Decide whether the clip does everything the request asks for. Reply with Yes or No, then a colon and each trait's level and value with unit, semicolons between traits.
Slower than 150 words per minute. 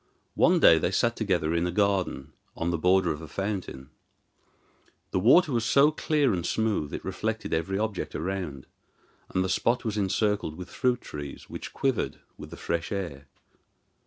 No: average, 170 wpm